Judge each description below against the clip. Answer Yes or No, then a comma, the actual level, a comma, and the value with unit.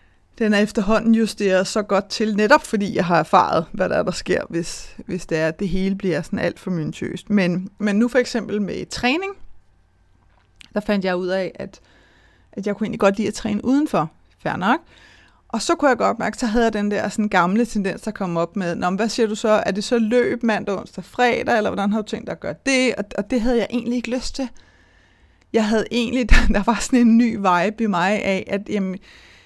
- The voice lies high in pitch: Yes, high, 210 Hz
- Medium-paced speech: No, fast, 230 wpm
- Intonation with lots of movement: No, average, 3.6 semitones